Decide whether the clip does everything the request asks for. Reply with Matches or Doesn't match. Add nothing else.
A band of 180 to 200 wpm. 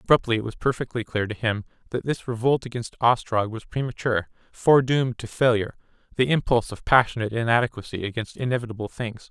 Doesn't match